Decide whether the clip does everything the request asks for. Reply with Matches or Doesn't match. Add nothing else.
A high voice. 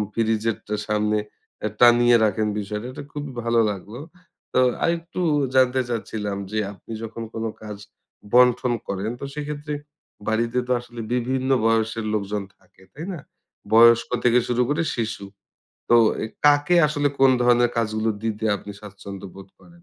Doesn't match